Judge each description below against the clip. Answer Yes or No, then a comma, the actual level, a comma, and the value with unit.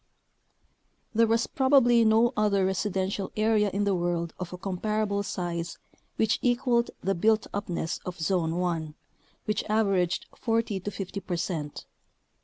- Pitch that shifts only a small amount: No, average, 3.6 semitones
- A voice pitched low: No, high, 200 Hz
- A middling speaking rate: Yes, average, 145 wpm